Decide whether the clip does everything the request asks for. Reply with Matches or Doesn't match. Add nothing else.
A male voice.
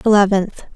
Doesn't match